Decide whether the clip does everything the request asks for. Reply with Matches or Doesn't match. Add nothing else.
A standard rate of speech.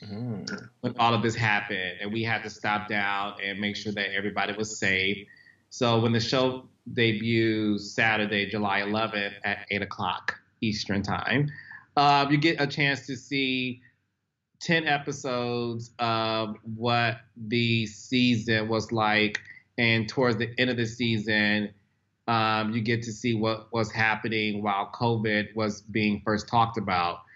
Matches